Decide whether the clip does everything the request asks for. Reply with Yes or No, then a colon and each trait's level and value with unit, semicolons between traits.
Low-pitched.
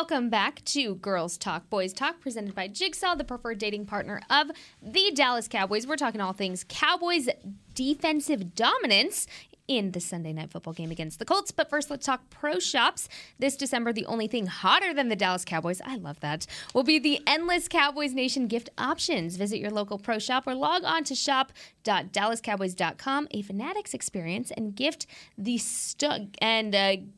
No: high, 235 Hz